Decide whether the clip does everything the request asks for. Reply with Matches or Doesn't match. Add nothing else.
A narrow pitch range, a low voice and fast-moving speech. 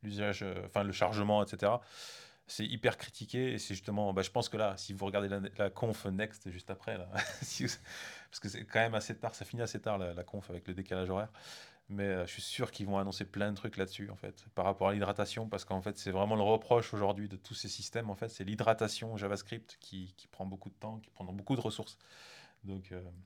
Matches